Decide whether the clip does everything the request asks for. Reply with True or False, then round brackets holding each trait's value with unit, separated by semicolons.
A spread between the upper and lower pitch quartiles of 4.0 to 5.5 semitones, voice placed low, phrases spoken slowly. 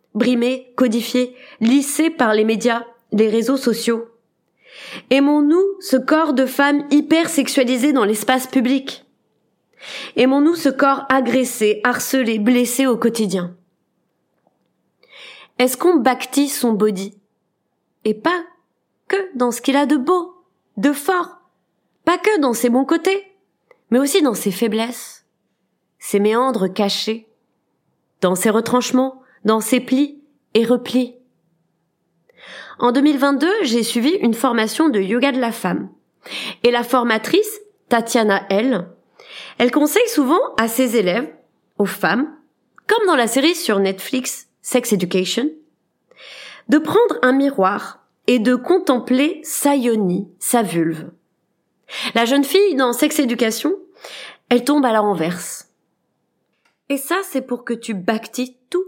False (4.5 semitones; 250 Hz; 130 wpm)